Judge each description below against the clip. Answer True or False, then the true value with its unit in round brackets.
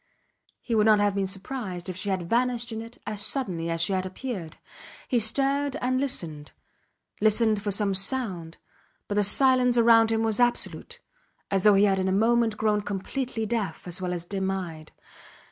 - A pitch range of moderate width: True (3.8 semitones)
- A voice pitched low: False (210 Hz)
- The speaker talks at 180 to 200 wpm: True (185 wpm)